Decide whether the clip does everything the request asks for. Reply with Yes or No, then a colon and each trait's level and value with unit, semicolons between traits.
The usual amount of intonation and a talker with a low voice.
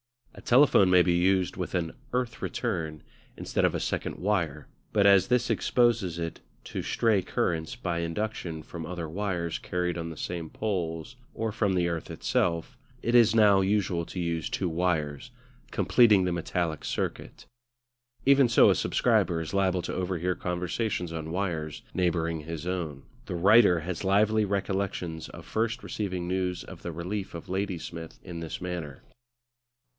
Yes: average, 3.2 semitones; very low, 90 Hz